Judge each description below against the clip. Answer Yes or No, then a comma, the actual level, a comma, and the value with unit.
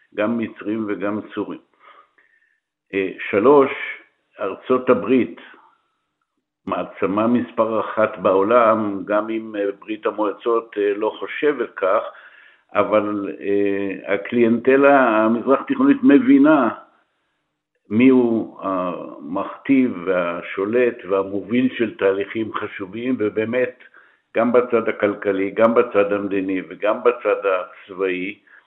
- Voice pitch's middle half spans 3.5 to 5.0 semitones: Yes, average, 4.5 semitones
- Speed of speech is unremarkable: No, slow, 85 wpm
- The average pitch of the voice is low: Yes, low, 110 Hz